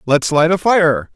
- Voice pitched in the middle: Yes, medium, 160 Hz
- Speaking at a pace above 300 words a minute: No, fast, 205 wpm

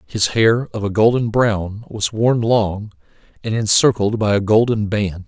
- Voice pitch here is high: No, low, 110 Hz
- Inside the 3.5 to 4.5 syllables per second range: Yes, 4.1 syllables/s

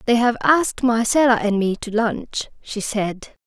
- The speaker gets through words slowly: No, average, 175 wpm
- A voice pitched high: Yes, high, 230 Hz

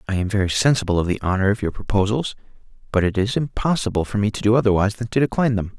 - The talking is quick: Yes, fast, 240 wpm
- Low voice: Yes, low, 105 Hz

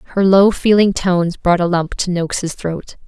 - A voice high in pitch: No, medium, 180 Hz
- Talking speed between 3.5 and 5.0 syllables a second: Yes, 4.8 syllables/s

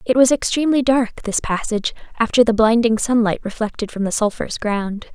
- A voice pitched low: No, high, 225 Hz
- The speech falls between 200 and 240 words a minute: No, average, 175 wpm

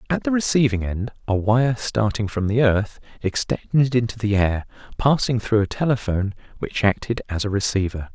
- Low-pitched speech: Yes, low, 110 Hz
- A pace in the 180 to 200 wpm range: No, average, 170 wpm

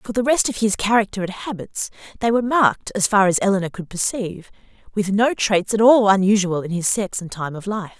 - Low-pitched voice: No, high, 205 Hz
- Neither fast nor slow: No, fast, 225 wpm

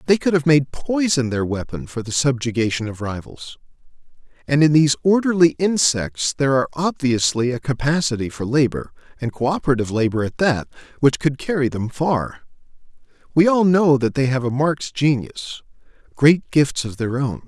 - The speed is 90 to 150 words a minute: No, average, 165 wpm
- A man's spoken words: Yes, male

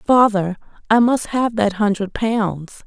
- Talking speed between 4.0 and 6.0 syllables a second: No, 3.7 syllables/s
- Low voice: No, high, 215 Hz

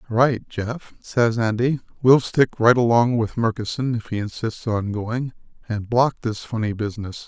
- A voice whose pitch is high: No, low, 115 Hz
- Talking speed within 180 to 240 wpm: No, average, 165 wpm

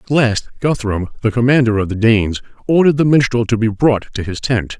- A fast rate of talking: Yes, fast, 215 wpm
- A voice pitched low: Yes, low, 115 Hz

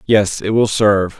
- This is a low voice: Yes, low, 105 Hz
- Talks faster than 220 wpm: No, average, 200 wpm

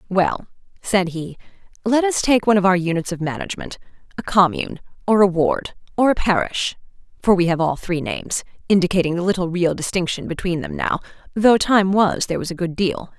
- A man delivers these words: No, female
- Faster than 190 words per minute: No, average, 185 wpm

